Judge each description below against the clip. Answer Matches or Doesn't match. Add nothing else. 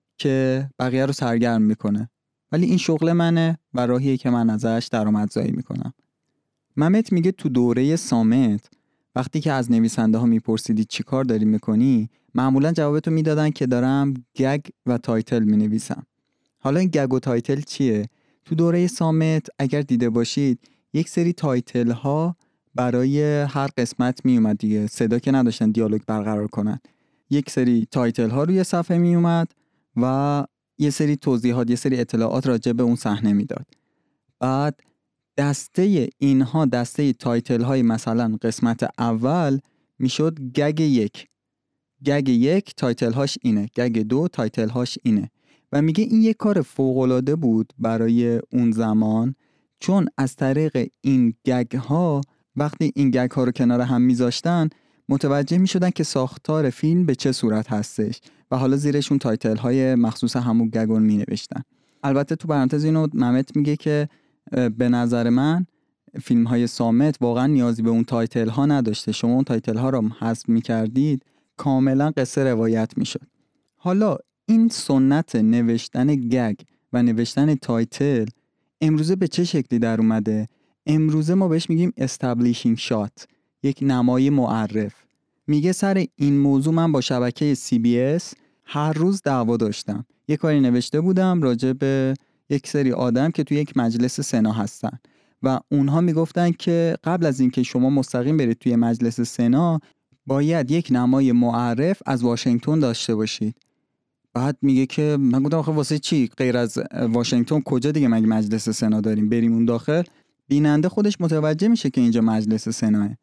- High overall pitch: Doesn't match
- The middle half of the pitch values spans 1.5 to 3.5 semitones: Doesn't match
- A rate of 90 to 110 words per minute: Doesn't match